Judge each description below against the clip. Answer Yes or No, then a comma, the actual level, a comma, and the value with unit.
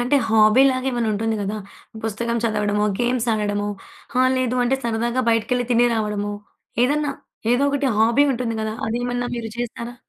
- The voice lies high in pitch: Yes, high, 235 Hz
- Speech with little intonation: Yes, narrow, 2.3 semitones